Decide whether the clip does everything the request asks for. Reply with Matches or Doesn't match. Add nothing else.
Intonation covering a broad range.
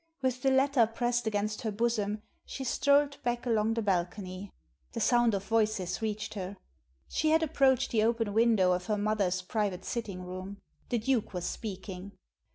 Doesn't match